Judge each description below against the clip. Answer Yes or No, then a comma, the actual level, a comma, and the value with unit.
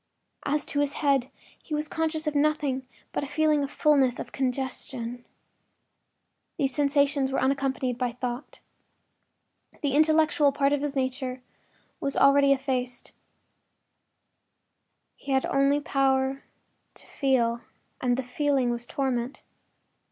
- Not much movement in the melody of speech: Yes, narrow, 1.9 semitones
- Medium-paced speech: No, slow, 120 wpm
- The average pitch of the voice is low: No, very high, 275 Hz